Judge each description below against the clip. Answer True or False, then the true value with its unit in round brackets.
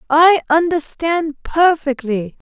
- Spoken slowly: True (70 wpm)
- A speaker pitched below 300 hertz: False (305 Hz)